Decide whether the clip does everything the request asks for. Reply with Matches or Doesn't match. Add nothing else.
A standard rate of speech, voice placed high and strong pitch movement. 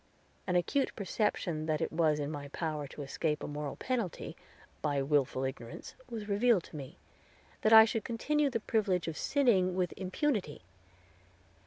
Doesn't match